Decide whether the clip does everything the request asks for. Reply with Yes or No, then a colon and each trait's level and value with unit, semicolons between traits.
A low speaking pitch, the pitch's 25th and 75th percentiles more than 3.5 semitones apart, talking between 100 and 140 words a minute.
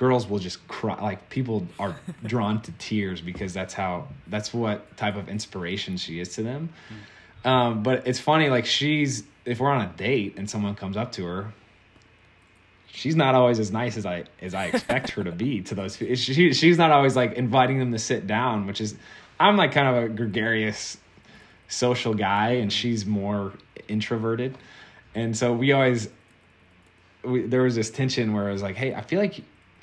No: low, 110 Hz; average, 3.9 semitones; average, 190 wpm